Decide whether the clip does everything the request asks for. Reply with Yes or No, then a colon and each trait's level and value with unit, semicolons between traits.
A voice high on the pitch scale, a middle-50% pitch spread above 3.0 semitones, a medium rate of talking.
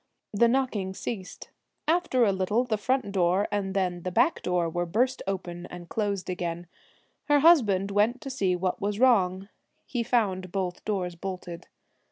Yes: high, 195 Hz; average, 4.5 semitones; average, 165 wpm